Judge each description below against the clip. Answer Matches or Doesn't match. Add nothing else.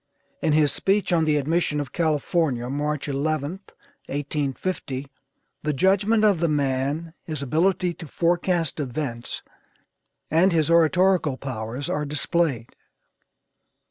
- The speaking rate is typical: Doesn't match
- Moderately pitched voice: Matches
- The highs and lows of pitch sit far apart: Doesn't match